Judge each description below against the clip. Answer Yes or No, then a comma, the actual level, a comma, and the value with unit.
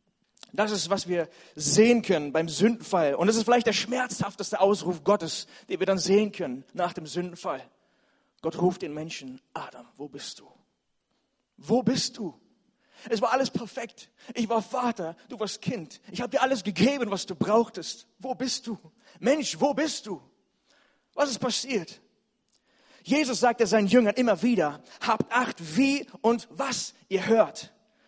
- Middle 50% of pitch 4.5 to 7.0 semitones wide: Yes, average, 4.9 semitones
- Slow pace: No, average, 160 wpm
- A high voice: Yes, high, 215 Hz